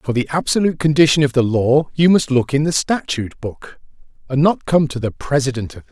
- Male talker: Yes, male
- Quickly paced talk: Yes, fast, 235 wpm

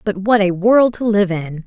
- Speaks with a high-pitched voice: Yes, high, 200 Hz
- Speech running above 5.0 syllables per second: No, 4.5 syllables/s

